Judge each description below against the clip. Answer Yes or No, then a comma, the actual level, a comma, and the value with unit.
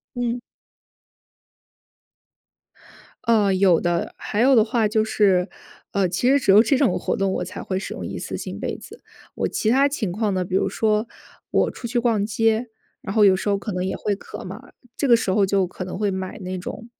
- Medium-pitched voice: No, high, 210 Hz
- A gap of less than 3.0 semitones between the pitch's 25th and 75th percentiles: No, average, 3.4 semitones